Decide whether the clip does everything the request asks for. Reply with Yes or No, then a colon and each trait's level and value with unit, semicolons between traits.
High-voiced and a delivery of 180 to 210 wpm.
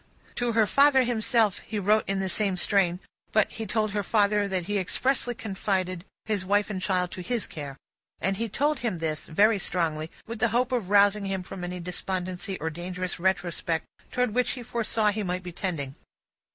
Yes: high, 200 Hz; average, 190 wpm